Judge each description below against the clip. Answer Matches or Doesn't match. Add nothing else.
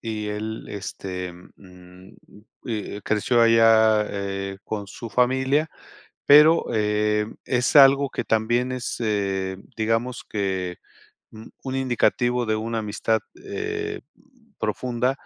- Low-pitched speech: Matches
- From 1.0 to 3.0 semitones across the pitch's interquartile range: Doesn't match